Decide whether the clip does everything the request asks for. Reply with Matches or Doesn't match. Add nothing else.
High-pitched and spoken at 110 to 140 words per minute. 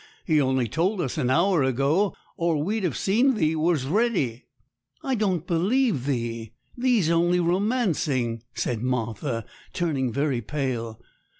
Doesn't match